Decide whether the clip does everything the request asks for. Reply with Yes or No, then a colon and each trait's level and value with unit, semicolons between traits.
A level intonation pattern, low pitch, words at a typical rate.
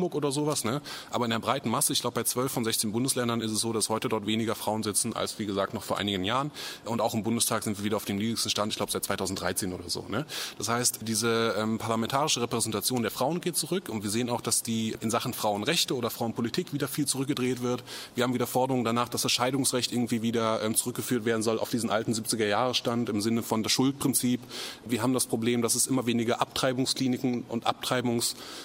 No: narrow, 2.2 semitones; low, 120 Hz; fast, 225 wpm